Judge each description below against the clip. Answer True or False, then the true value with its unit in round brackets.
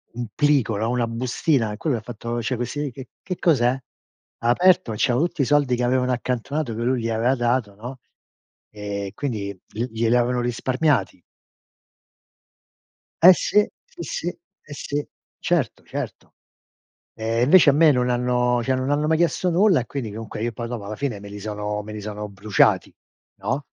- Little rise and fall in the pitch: False (4.0 semitones)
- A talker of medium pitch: False (125 Hz)